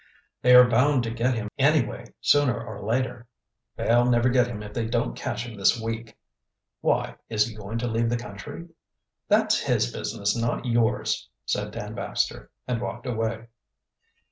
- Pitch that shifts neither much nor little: No, narrow, 1.7 semitones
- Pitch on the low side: Yes, low, 115 Hz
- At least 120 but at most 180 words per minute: Yes, average, 170 wpm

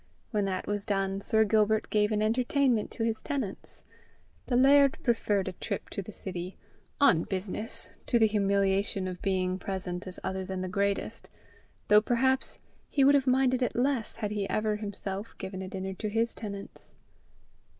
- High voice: Yes, high, 210 Hz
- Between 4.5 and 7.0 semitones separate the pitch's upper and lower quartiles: No, average, 3.3 semitones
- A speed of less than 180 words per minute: Yes, average, 170 wpm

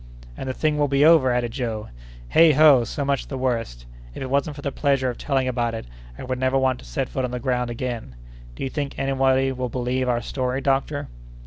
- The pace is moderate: No, fast, 230 wpm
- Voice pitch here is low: Yes, low, 130 Hz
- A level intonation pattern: Yes, narrow, 1.9 semitones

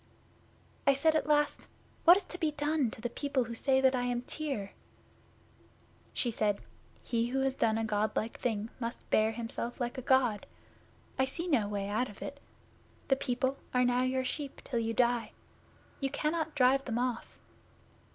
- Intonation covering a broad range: No, average, 3.3 semitones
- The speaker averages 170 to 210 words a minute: Yes, average, 180 wpm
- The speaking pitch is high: Yes, very high, 250 Hz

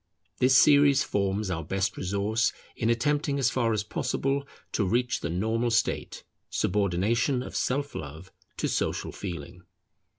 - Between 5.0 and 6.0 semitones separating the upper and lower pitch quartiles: Yes, average, 5.3 semitones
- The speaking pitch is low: Yes, low, 110 Hz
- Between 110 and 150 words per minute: Yes, average, 140 wpm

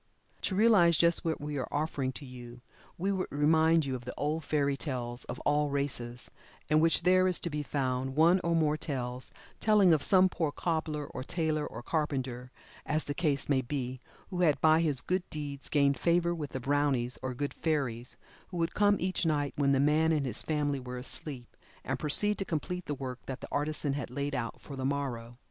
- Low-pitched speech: No, medium, 145 Hz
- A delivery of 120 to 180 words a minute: No, fast, 205 wpm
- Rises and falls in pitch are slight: No, average, 3.7 semitones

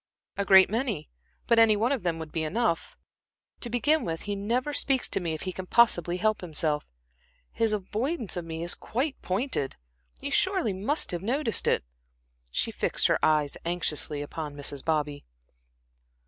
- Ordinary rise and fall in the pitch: No, wide, 6.4 semitones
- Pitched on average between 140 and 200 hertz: Yes, high, 190 Hz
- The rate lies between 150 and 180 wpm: Yes, average, 170 wpm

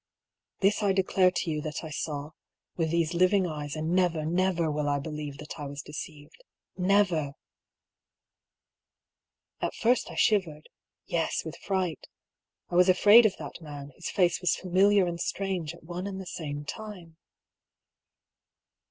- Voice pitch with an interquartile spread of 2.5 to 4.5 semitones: Yes, average, 3.8 semitones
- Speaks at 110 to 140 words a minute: No, average, 160 wpm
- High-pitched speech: No, medium, 170 Hz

